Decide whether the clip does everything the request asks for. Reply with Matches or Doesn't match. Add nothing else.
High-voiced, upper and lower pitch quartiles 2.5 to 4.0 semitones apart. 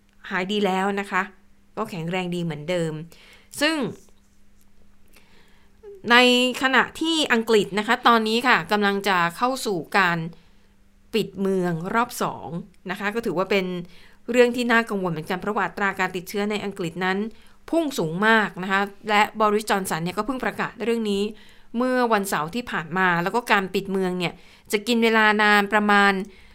Matches